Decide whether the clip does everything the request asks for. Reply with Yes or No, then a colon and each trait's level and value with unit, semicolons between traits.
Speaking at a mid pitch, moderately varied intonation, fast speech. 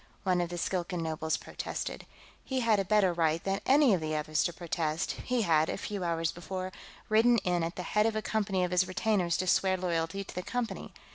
Yes: medium, 180 Hz; average, 3.8 semitones; fast, 220 wpm